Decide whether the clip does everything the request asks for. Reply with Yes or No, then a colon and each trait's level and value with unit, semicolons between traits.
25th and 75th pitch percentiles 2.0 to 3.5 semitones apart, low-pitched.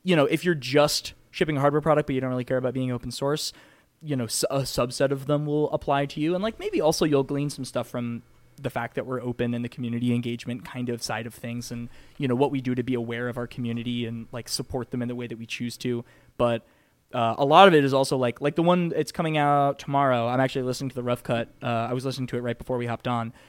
Yes: average, 3.1 semitones; low, 130 Hz